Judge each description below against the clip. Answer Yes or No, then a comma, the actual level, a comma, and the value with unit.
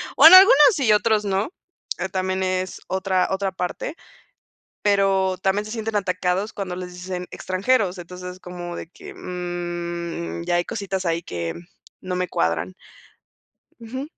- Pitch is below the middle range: No, medium, 185 Hz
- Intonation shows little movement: Yes, narrow, 2.3 semitones